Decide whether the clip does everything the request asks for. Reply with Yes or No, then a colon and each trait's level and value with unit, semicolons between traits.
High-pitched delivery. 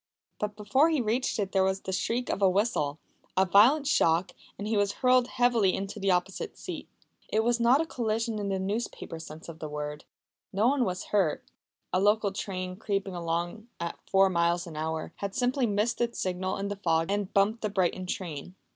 Yes: high, 200 Hz